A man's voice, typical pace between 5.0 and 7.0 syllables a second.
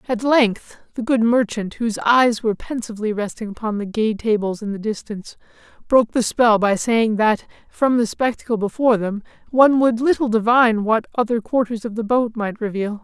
Yes: male; 5.4 syllables/s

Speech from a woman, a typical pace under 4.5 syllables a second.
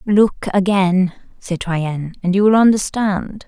Yes: female; 4.1 syllables/s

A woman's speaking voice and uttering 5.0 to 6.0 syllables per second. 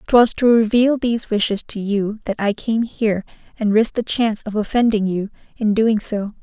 Yes: female; 5.3 syllables/s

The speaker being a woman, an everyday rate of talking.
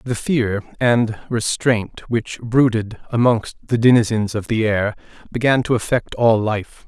No: male; average, 150 wpm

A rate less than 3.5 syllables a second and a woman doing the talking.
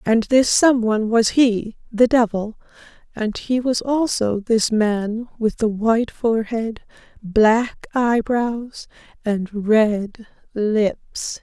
Yes: 3.2 syllables/s; female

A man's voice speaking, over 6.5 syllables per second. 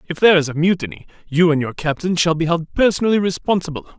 Yes: male; 6.8 syllables/s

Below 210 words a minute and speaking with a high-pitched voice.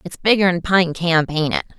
No: average, 200 wpm; medium, 175 Hz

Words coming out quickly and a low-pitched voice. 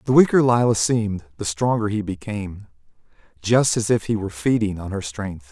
No: average, 185 wpm; low, 105 Hz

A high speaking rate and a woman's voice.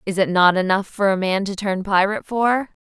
Yes: fast, 230 wpm; female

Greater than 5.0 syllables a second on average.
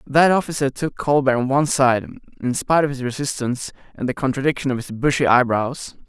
Yes: 6.0 syllables/s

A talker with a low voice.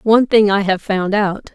No: high, 205 Hz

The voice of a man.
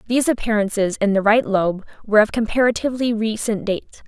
No: female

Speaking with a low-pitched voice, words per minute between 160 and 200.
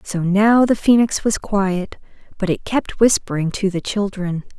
No: high, 200 Hz; average, 170 wpm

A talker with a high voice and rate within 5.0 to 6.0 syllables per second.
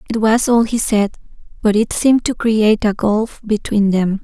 No: high, 215 Hz; 4.8 syllables/s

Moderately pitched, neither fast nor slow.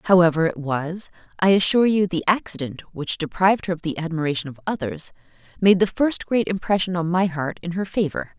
Yes: medium, 175 Hz; average, 195 wpm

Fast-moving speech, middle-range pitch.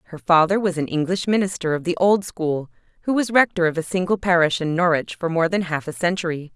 Yes: fast, 230 wpm; medium, 175 Hz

